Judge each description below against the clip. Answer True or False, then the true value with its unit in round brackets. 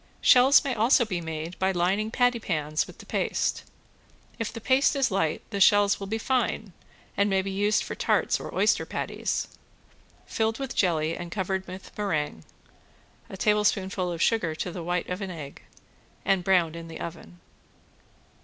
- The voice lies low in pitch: False (190 Hz)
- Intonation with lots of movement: False (4.0 semitones)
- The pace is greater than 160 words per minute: True (170 wpm)